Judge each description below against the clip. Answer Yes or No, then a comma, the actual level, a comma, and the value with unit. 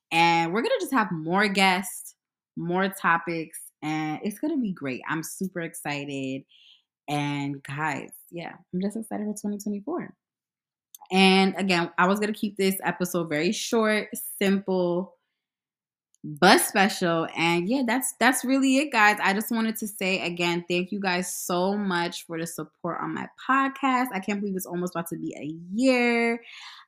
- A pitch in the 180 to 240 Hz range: Yes, medium, 185 Hz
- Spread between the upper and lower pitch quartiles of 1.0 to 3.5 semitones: No, average, 4.0 semitones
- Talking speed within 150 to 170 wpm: Yes, average, 160 wpm